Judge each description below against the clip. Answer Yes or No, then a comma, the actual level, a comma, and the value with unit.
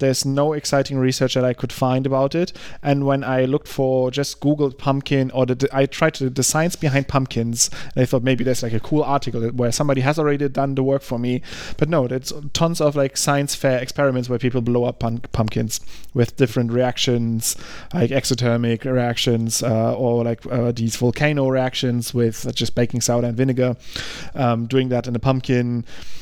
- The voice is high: No, low, 130 Hz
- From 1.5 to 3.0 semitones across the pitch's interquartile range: Yes, narrow, 2.4 semitones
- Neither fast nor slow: Yes, average, 195 wpm